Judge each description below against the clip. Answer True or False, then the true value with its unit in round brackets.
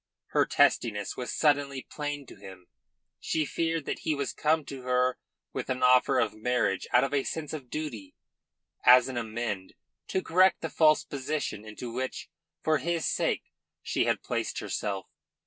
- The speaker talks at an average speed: True (165 wpm)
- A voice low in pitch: True (130 Hz)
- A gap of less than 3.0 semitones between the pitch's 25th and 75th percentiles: False (4.3 semitones)